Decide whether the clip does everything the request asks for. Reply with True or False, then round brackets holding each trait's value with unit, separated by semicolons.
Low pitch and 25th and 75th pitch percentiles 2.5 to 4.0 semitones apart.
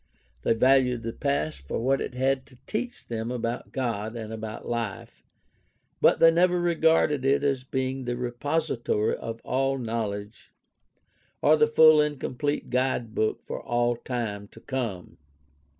True (125 Hz; 3.4 semitones)